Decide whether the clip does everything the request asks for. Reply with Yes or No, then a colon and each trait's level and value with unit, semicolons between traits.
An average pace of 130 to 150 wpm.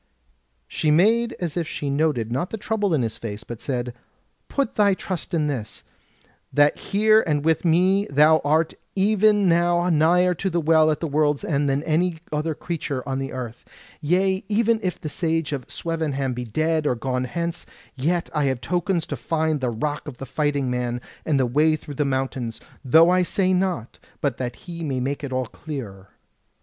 No: average, 190 wpm